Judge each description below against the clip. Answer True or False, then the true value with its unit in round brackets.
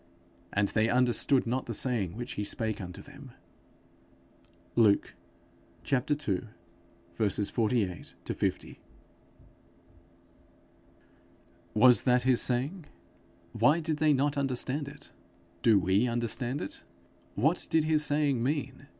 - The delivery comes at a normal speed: False (105 wpm)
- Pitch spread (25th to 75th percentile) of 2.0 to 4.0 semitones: False (4.5 semitones)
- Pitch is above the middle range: False (125 Hz)